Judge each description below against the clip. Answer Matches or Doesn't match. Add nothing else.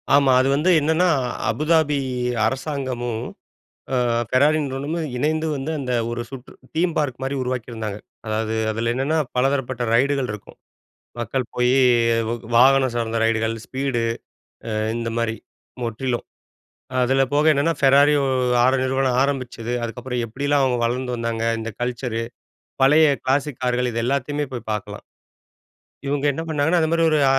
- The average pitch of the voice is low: Matches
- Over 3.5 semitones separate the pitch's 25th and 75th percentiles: Doesn't match